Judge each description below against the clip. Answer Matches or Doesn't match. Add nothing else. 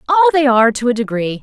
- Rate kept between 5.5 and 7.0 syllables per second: Matches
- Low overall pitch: Doesn't match